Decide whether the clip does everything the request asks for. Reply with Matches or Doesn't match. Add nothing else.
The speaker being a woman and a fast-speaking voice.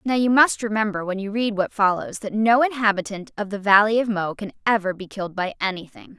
Matches